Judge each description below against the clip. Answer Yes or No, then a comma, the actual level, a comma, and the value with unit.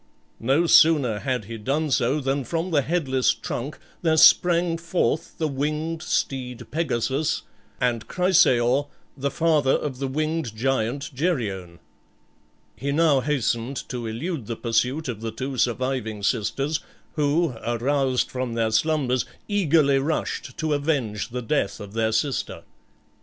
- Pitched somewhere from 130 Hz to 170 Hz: Yes, low, 135 Hz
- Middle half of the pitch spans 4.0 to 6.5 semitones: Yes, average, 4.6 semitones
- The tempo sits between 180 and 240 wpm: No, slow, 135 wpm